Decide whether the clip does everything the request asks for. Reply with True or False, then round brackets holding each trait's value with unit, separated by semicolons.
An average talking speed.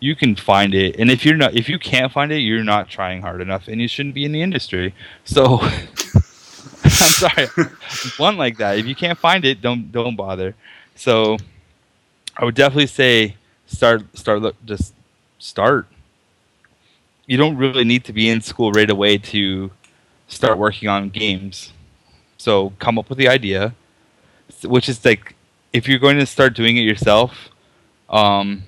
True (175 wpm)